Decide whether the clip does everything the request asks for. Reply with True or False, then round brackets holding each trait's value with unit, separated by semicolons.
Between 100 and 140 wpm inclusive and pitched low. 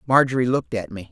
False (215 wpm; 115 Hz)